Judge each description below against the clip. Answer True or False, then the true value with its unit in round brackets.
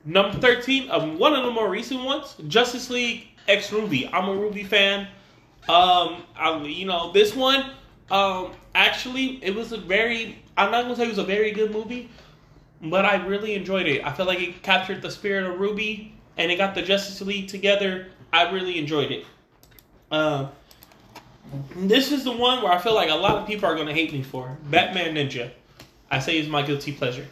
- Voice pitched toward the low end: False (195 Hz)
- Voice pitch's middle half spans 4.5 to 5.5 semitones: True (5.1 semitones)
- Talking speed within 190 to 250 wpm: True (200 wpm)